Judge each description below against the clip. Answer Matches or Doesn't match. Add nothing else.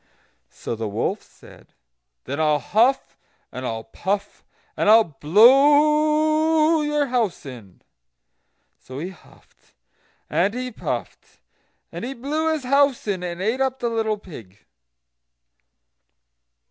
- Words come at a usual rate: Doesn't match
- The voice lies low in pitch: Doesn't match